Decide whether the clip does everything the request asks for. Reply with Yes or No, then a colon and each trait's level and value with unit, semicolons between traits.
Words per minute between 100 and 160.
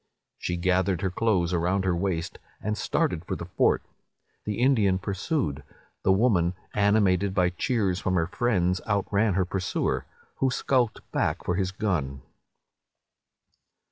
Yes: average, 140 wpm